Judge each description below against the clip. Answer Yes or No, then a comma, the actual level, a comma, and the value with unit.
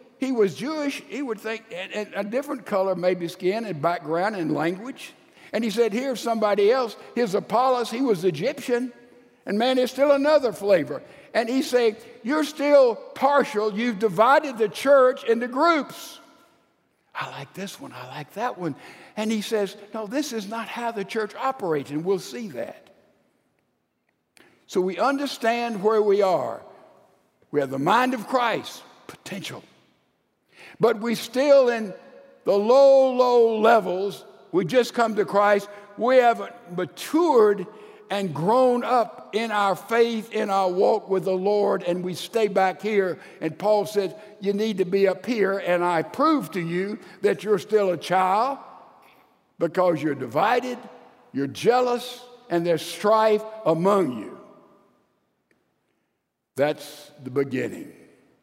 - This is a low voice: No, high, 220 Hz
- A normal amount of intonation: Yes, average, 4.5 semitones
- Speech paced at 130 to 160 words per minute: Yes, average, 150 wpm